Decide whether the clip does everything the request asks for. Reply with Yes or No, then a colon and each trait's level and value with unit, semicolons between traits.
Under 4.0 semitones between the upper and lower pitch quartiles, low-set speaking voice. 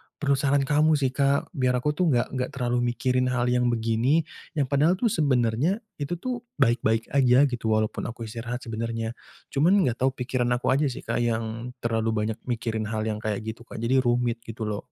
Yes: average, 3.3 semitones; low, 125 Hz